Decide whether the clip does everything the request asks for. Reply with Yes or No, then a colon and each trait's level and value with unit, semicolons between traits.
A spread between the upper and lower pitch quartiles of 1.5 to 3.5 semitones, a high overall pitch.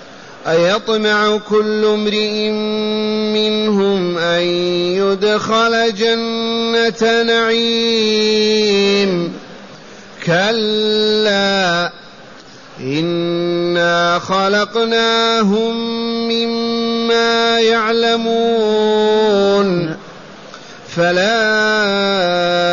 Yes: average, 3.2 semitones; high, 215 Hz